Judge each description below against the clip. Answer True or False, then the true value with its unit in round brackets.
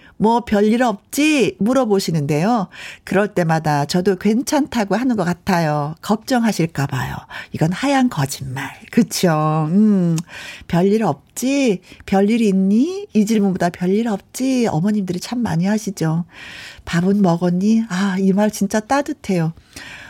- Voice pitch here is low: False (195 Hz)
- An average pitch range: True (4.5 semitones)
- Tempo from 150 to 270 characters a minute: True (265 characters per minute)